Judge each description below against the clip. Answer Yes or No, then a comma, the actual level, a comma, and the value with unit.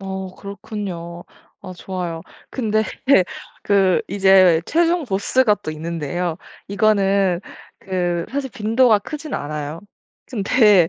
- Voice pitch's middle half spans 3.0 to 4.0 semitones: Yes, average, 3.6 semitones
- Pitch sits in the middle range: No, high, 195 Hz